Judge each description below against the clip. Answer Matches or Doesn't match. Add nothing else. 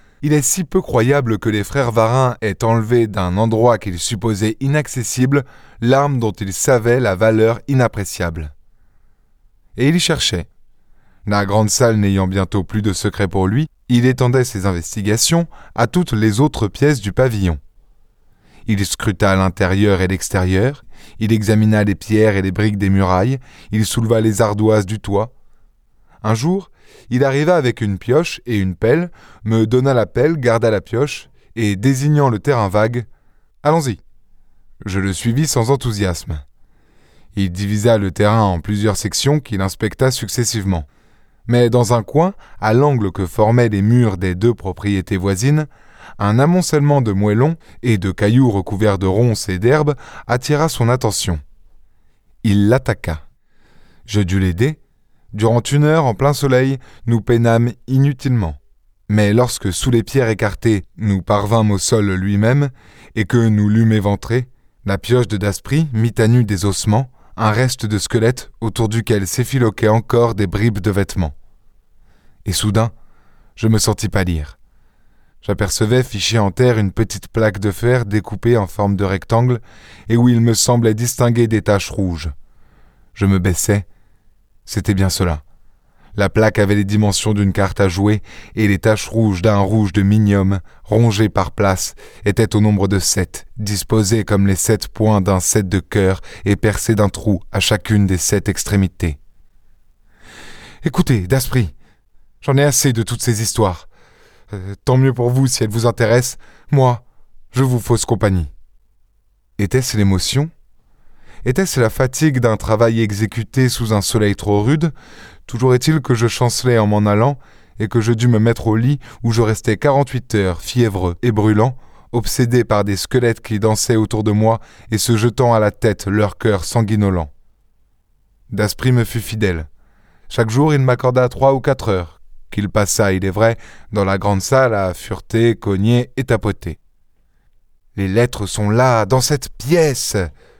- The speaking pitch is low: Matches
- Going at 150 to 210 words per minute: Matches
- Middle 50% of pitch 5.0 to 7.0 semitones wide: Doesn't match